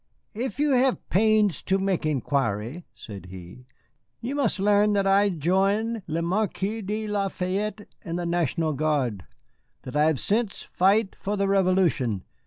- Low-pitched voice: No, high, 190 Hz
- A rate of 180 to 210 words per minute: No, average, 155 wpm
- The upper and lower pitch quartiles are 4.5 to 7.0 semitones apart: Yes, average, 5.2 semitones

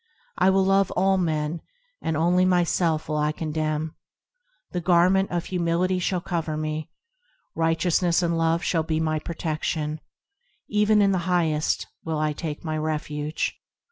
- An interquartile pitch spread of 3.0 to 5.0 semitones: No, narrow, 2.6 semitones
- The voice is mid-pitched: Yes, medium, 165 Hz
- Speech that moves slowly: No, average, 145 wpm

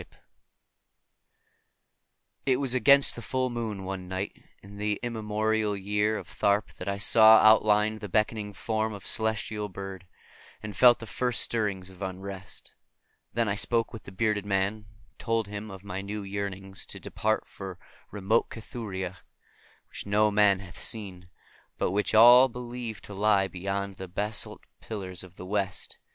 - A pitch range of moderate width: No, narrow, 2.2 semitones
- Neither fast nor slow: Yes, average, 165 wpm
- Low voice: Yes, low, 105 Hz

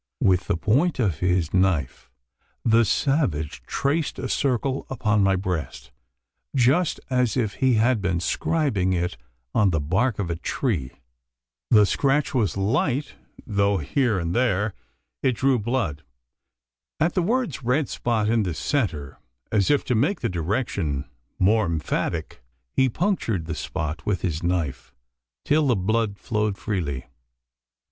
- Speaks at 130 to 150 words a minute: Yes, average, 145 wpm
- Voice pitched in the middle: No, low, 105 Hz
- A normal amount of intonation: No, wide, 6.6 semitones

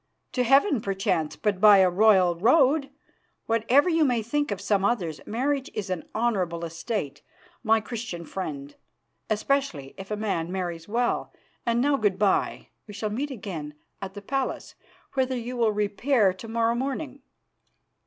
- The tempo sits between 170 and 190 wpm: No, average, 155 wpm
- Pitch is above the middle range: Yes, high, 215 Hz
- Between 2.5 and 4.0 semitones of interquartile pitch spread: No, average, 5.1 semitones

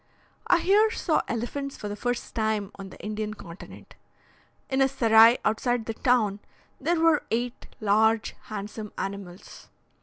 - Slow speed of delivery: No, average, 145 wpm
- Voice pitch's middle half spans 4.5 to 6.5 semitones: No, average, 3.3 semitones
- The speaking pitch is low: No, high, 225 Hz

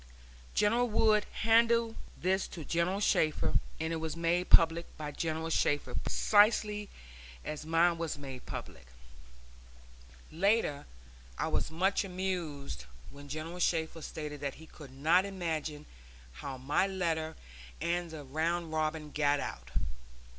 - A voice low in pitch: No, medium, 165 Hz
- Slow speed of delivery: Yes, slow, 130 wpm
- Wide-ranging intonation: No, average, 3.7 semitones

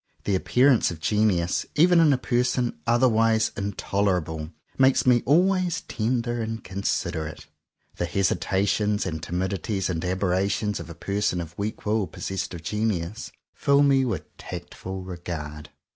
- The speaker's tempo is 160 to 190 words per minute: No, average, 140 wpm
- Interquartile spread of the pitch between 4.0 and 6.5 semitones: Yes, average, 5.1 semitones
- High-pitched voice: No, low, 100 Hz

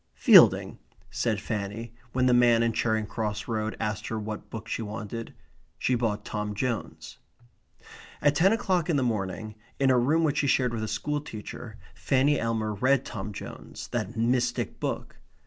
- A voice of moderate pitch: No, low, 115 Hz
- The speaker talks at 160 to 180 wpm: Yes, average, 170 wpm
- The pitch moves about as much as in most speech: Yes, average, 3.1 semitones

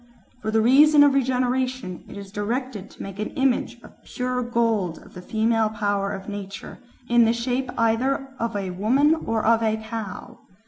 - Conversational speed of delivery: Yes, average, 180 wpm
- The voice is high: Yes, high, 230 Hz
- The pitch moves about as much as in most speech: Yes, average, 3.7 semitones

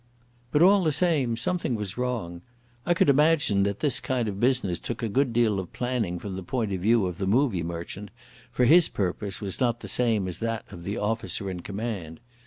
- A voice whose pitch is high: No, low, 115 Hz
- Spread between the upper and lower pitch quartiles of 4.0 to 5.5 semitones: Yes, average, 4.8 semitones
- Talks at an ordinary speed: No, fast, 210 wpm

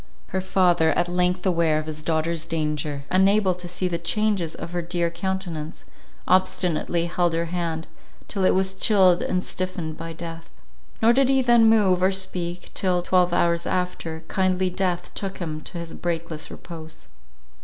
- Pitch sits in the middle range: Yes, medium, 175 Hz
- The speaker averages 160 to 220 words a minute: Yes, average, 165 wpm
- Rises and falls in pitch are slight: Yes, narrow, 2.1 semitones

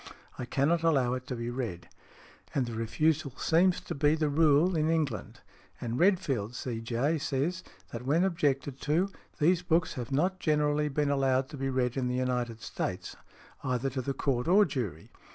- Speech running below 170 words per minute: No, average, 175 wpm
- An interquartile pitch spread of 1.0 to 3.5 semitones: No, average, 4.4 semitones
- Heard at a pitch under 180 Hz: Yes, medium, 140 Hz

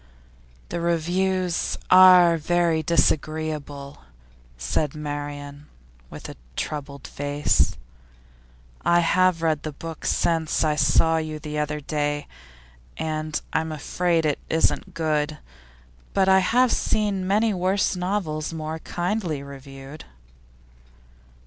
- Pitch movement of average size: Yes, average, 3.0 semitones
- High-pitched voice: No, medium, 160 Hz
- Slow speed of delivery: Yes, slow, 110 wpm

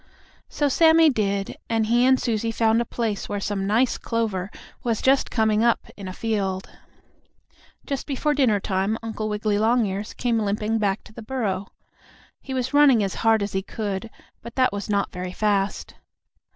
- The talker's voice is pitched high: Yes, high, 220 Hz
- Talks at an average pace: Yes, average, 175 wpm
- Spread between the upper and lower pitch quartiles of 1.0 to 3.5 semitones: Yes, average, 2.9 semitones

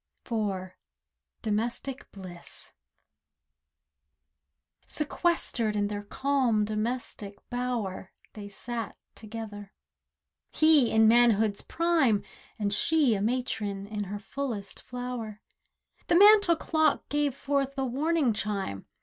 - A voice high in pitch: Yes, high, 230 Hz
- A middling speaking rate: No, slow, 100 wpm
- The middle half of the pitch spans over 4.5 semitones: Yes, average, 5.0 semitones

